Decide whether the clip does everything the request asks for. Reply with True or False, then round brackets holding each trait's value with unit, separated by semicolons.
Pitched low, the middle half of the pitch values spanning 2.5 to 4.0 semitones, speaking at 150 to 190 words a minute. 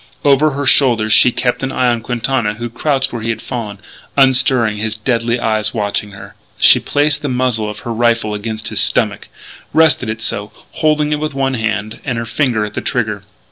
False (120 Hz; 3.6 semitones; 200 wpm)